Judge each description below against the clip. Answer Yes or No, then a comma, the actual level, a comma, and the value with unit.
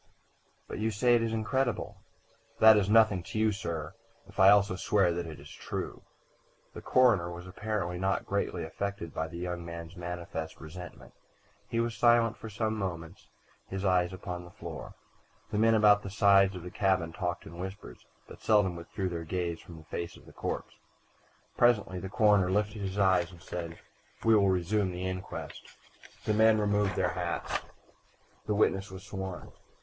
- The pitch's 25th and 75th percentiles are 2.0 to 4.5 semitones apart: Yes, average, 3.2 semitones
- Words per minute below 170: No, average, 175 wpm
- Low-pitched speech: Yes, very low, 95 Hz